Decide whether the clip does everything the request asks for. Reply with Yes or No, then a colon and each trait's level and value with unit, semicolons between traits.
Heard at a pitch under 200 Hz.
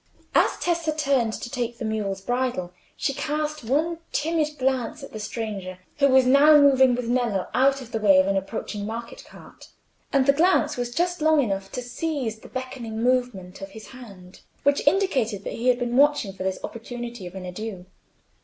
No: high, 245 Hz